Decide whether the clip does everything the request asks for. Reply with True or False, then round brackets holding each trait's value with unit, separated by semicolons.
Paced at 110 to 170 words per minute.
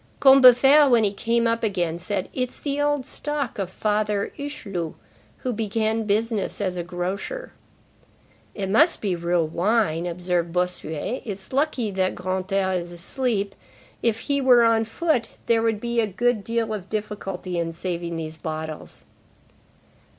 True (145 wpm)